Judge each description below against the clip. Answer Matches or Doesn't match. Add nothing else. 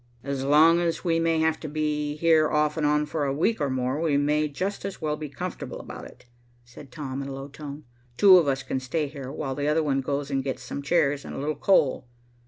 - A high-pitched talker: Doesn't match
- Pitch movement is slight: Matches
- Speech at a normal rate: Doesn't match